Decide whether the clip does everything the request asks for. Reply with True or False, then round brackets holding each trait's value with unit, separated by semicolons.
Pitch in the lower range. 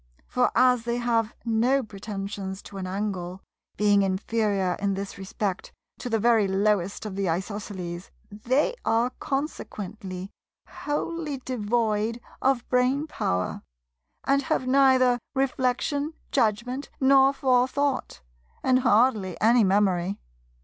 False (225 Hz)